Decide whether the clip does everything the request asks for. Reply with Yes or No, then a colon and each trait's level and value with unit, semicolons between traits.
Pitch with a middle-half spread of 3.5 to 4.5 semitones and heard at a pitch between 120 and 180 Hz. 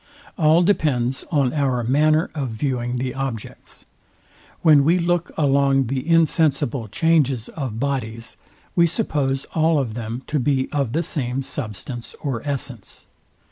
Yes: average, 3.9 semitones; low, 135 Hz